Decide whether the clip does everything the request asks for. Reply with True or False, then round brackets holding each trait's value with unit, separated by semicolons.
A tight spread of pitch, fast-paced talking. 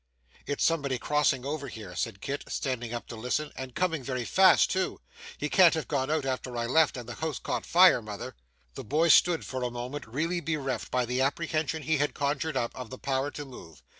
False (4.0 semitones; 215 wpm)